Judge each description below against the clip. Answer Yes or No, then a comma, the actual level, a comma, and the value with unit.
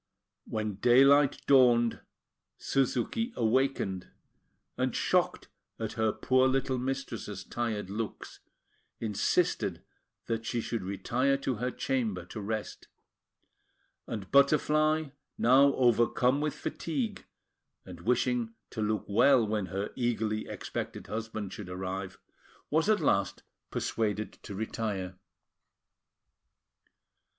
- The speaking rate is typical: No, slow, 105 wpm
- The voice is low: Yes, low, 115 Hz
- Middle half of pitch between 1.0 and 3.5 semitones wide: No, average, 4.1 semitones